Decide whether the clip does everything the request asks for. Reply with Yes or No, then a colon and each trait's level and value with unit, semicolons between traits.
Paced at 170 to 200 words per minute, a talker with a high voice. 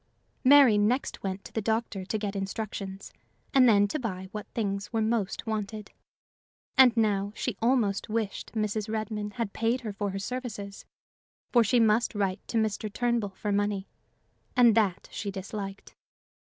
No: average, 160 wpm; high, 215 Hz